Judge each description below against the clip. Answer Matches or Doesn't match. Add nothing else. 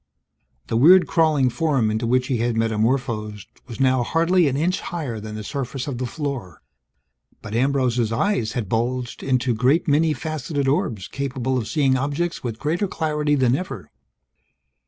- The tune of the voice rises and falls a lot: Doesn't match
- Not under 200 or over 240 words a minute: Doesn't match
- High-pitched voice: Doesn't match